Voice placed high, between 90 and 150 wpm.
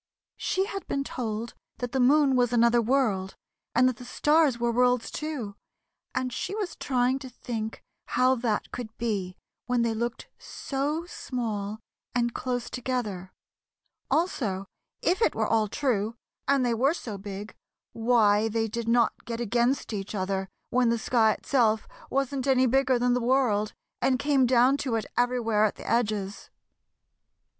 No: high, 240 Hz; average, 160 wpm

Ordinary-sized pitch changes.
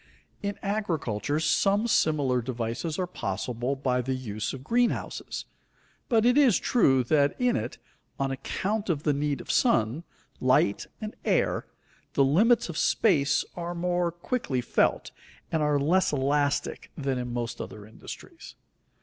No: wide, 6.6 semitones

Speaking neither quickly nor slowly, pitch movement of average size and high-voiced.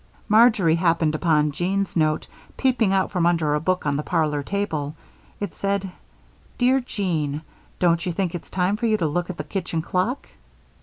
No: average, 175 wpm; average, 4.1 semitones; medium, 175 Hz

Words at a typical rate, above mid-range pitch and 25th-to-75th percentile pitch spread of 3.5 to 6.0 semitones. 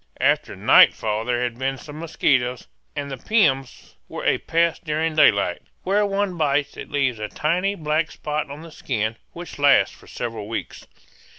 No: average, 170 wpm; medium, 145 Hz; average, 4.8 semitones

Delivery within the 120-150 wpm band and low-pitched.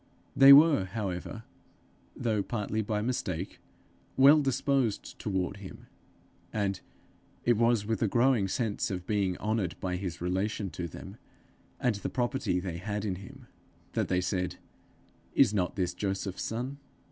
Yes: average, 145 wpm; low, 105 Hz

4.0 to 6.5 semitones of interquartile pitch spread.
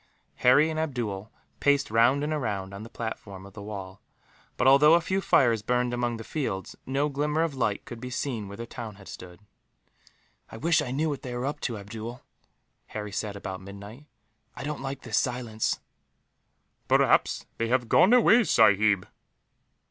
Yes: average, 5.1 semitones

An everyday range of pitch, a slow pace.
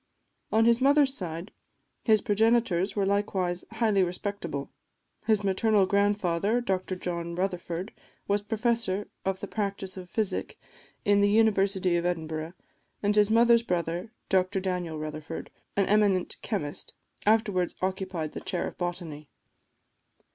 Yes: average, 3.1 semitones; slow, 130 wpm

